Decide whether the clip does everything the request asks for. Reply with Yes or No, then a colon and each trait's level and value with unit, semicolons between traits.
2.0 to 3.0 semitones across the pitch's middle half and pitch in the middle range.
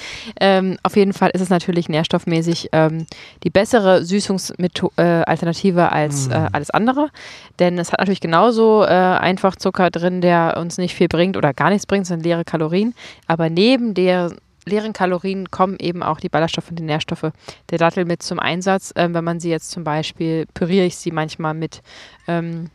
Yes: narrow, 2.4 semitones; medium, 175 Hz